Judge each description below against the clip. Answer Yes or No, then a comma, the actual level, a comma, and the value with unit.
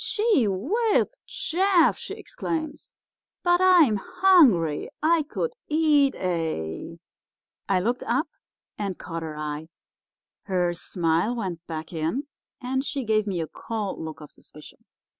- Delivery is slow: Yes, slow, 130 wpm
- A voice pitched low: No, high, 220 Hz